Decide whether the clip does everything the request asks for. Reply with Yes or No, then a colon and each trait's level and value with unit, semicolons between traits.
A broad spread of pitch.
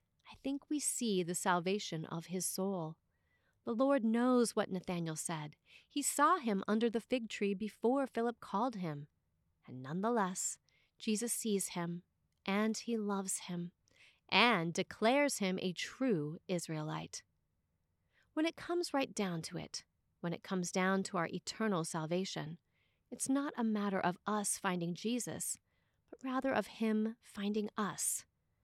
No: average, 5.0 semitones